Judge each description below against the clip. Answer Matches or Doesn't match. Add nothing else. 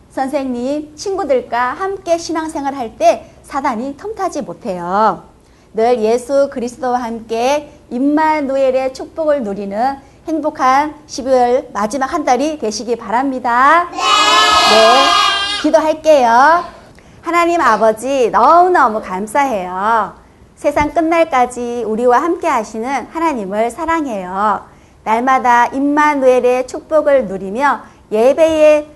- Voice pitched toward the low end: Doesn't match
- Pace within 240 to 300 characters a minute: Matches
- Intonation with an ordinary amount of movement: Matches